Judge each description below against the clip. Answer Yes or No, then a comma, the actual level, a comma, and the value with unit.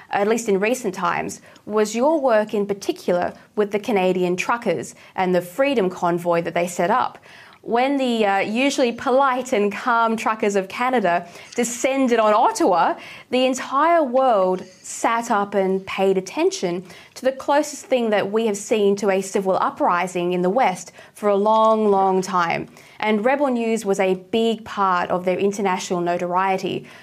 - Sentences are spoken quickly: No, average, 165 wpm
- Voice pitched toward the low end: No, high, 205 Hz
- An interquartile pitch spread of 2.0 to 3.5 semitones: No, average, 4.6 semitones